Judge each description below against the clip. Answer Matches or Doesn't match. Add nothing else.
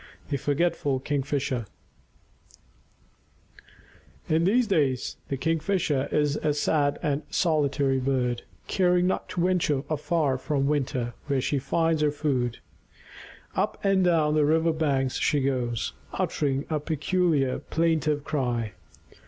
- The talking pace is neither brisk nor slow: Doesn't match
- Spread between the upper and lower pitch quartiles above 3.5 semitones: Doesn't match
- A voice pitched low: Doesn't match